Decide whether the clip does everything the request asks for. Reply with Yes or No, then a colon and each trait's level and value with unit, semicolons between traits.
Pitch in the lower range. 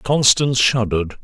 Yes: low, 120 Hz